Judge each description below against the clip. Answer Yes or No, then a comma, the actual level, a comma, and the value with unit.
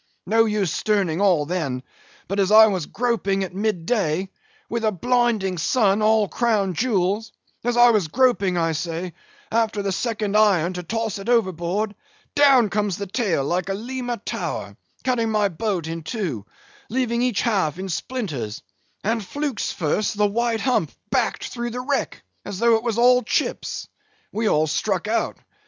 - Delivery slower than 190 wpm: Yes, average, 165 wpm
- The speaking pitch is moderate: No, high, 210 Hz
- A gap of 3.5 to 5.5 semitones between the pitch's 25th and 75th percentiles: Yes, average, 4.3 semitones